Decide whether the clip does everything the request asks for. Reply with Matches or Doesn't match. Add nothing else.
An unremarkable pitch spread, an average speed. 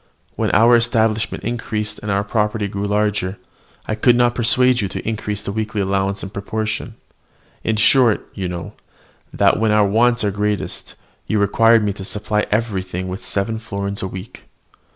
Doesn't match